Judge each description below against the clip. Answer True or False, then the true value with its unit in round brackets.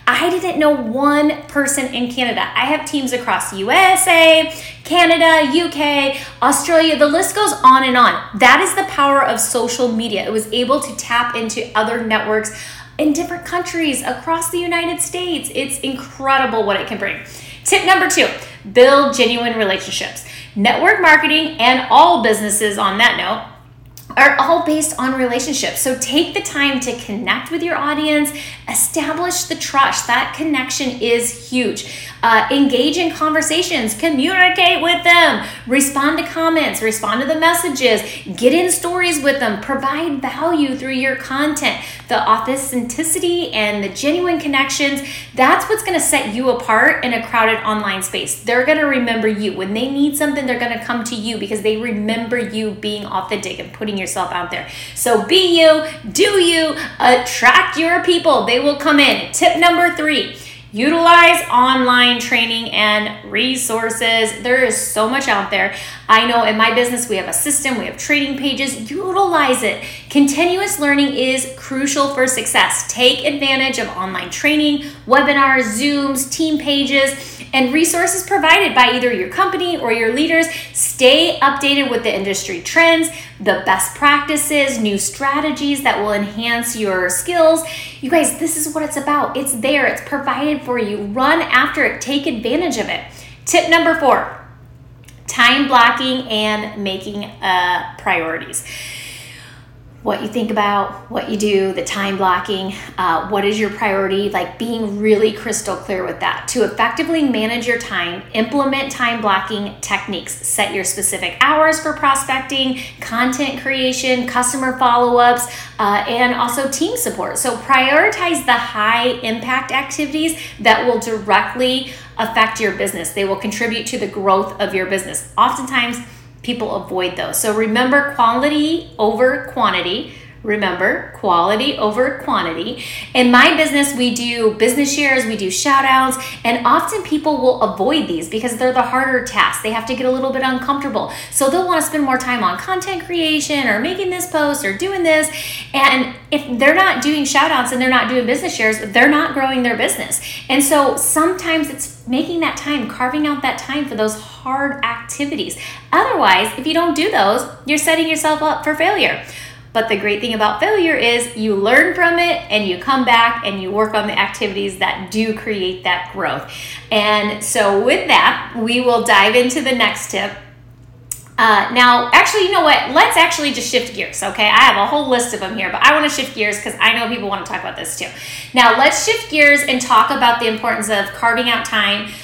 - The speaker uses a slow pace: False (170 wpm)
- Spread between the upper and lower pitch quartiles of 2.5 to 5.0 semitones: False (5.4 semitones)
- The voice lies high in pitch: True (255 Hz)